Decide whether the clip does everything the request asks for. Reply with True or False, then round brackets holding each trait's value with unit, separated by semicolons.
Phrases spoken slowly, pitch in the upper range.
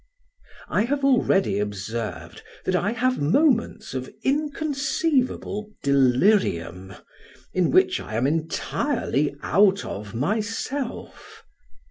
True (95 wpm; 200 Hz)